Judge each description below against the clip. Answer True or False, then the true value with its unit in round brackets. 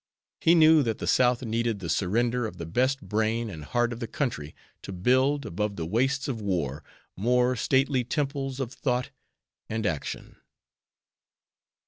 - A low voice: True (120 Hz)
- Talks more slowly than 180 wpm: True (155 wpm)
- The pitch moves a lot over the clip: False (4.3 semitones)